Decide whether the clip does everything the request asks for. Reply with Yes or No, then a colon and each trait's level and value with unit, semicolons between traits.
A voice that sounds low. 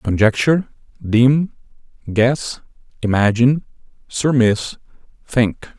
Yes: low, 120 Hz